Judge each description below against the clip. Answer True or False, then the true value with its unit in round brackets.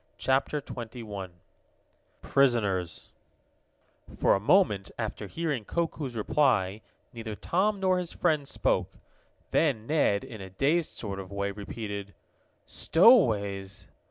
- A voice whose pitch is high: False (115 Hz)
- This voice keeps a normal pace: False (110 wpm)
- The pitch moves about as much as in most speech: False (7.2 semitones)